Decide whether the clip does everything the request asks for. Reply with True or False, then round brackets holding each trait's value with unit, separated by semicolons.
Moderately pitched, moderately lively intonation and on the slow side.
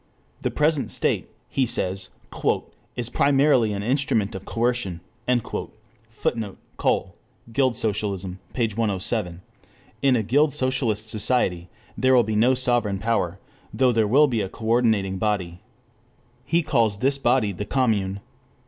False (110 Hz; 4.3 semitones; 130 wpm)